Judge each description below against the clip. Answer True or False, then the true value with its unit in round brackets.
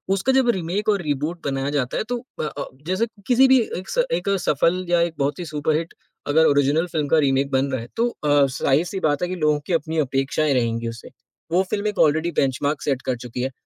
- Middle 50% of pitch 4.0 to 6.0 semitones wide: True (4.7 semitones)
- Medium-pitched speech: True (155 Hz)